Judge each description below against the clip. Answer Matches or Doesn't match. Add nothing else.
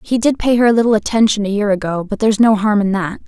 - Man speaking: Doesn't match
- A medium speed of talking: Doesn't match